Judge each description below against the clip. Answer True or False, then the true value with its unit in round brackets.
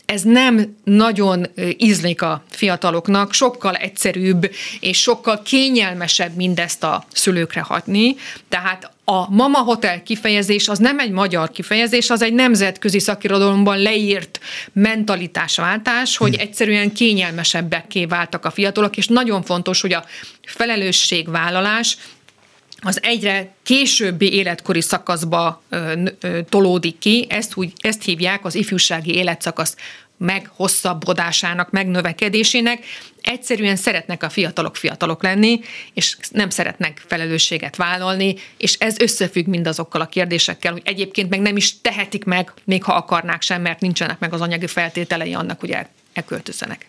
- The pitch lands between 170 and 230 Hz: True (190 Hz)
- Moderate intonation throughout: True (3.3 semitones)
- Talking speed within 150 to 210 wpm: False (125 wpm)